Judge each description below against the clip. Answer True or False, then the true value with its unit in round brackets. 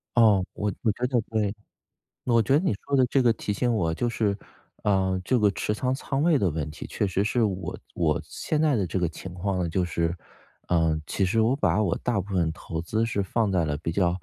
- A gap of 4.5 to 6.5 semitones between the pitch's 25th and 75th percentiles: True (4.9 semitones)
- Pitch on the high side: False (100 Hz)